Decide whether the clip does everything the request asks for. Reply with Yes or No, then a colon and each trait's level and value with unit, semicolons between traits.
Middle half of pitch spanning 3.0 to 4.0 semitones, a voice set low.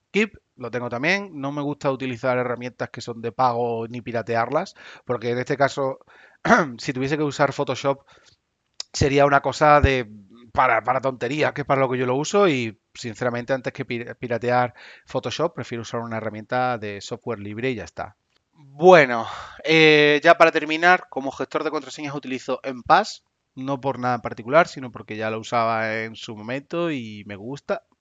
Yes: average, 3.4 semitones; low, 130 Hz